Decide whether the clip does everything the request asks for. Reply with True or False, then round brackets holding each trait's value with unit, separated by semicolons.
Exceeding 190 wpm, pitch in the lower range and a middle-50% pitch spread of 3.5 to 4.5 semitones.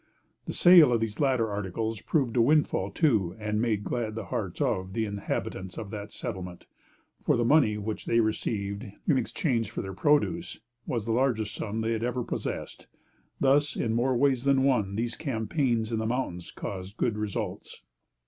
False (175 wpm; 115 Hz; 3.9 semitones)